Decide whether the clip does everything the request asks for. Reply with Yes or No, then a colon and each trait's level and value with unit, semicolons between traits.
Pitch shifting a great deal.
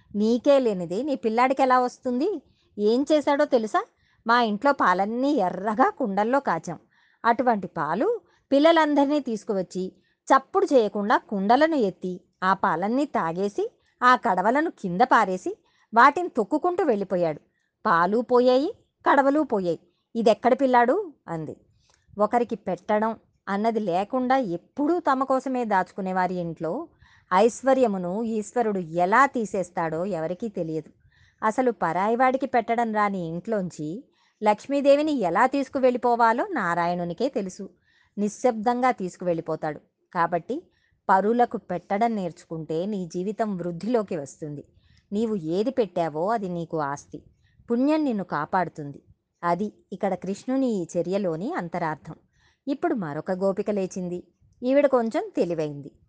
Yes: wide, 6.4 semitones